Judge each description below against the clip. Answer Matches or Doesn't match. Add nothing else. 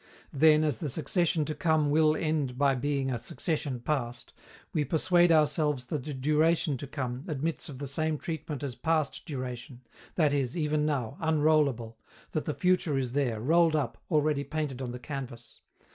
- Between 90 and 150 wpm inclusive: Doesn't match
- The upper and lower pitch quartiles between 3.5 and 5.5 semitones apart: Doesn't match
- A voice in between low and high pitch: Matches